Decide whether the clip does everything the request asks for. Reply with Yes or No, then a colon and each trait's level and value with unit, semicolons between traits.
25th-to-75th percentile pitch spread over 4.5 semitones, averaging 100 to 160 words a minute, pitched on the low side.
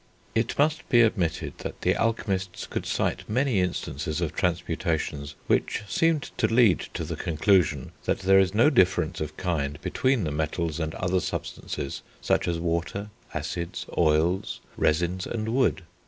Yes: average, 5.1 semitones; average, 155 wpm; very low, 90 Hz